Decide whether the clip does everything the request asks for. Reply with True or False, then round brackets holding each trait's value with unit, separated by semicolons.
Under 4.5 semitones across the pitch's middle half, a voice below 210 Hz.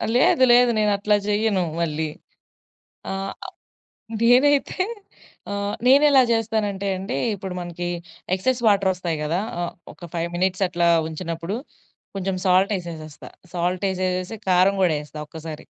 True (3.5 semitones; 185 Hz)